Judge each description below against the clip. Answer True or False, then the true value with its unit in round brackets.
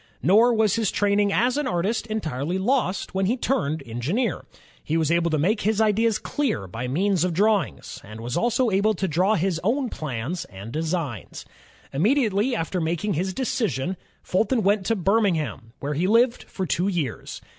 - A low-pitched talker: False (190 Hz)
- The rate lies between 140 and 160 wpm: False (175 wpm)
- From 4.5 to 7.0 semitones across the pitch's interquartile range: True (5.5 semitones)